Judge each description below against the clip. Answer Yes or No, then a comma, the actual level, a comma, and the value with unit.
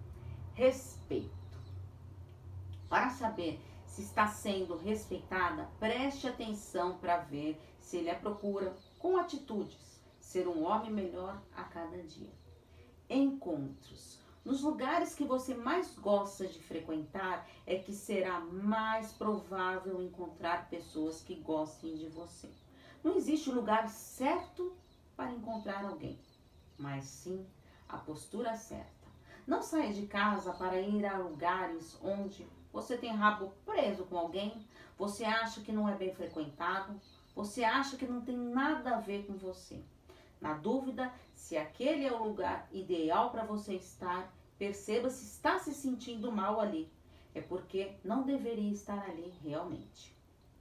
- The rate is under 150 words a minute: Yes, average, 135 wpm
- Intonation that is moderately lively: Yes, average, 4.9 semitones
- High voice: Yes, high, 195 Hz